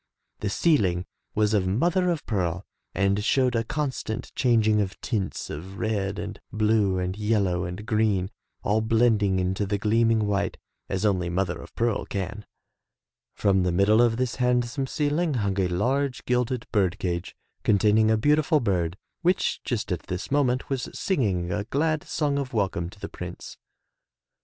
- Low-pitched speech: Yes, low, 105 Hz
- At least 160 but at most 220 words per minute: Yes, average, 165 wpm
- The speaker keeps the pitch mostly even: No, average, 4.3 semitones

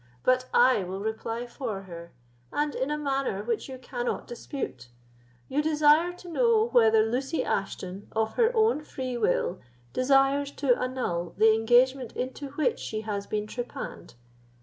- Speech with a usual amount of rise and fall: Yes, average, 4.6 semitones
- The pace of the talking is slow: No, average, 150 wpm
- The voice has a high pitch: Yes, very high, 250 Hz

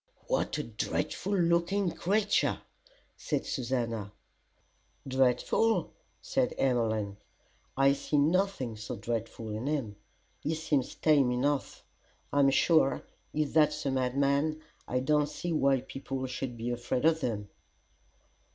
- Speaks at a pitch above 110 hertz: Yes, low, 135 Hz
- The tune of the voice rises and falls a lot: No, average, 4.1 semitones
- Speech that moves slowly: Yes, slow, 120 wpm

